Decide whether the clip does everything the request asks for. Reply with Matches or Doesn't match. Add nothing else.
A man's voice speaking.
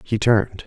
Matches